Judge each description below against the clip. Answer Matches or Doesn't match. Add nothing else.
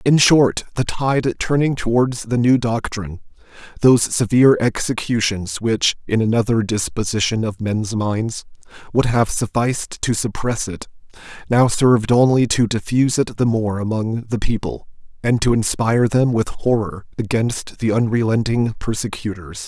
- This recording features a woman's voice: Doesn't match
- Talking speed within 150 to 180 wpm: Doesn't match